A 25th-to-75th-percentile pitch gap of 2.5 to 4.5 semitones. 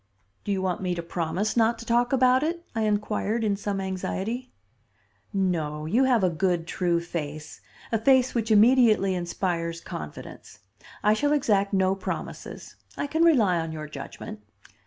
No: average, 5.3 semitones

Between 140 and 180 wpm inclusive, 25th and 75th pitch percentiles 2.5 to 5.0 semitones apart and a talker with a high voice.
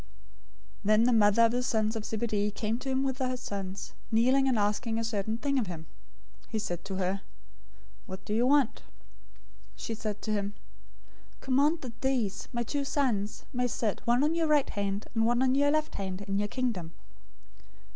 No: average, 195 wpm; average, 4.0 semitones; high, 225 Hz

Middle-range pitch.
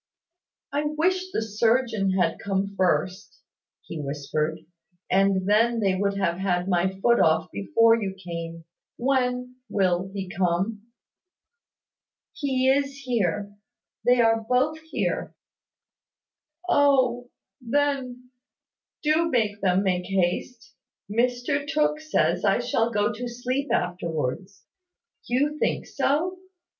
No: high, 225 Hz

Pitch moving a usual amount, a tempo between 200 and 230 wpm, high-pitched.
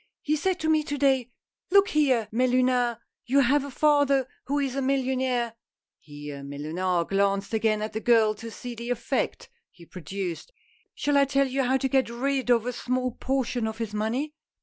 Yes: average, 3.9 semitones; fast, 205 wpm; very high, 250 Hz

